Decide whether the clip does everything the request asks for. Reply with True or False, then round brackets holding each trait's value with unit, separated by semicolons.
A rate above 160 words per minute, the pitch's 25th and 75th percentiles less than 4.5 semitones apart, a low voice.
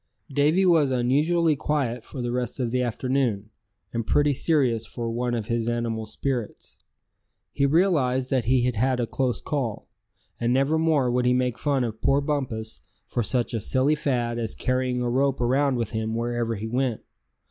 True (180 wpm; 2.8 semitones; 125 Hz)